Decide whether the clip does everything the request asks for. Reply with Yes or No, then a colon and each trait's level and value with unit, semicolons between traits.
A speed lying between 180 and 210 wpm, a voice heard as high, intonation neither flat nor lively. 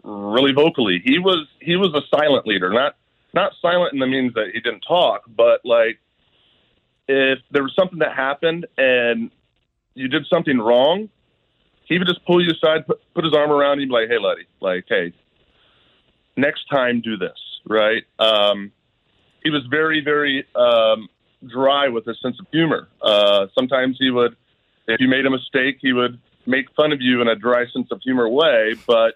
No: average, 185 wpm; low, 135 Hz; average, 4.6 semitones